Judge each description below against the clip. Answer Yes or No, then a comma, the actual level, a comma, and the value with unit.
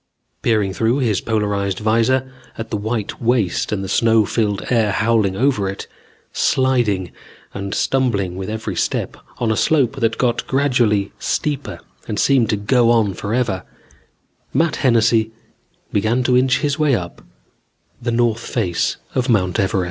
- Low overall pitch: Yes, low, 115 Hz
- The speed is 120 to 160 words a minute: Yes, average, 150 wpm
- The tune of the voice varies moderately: Yes, average, 3.5 semitones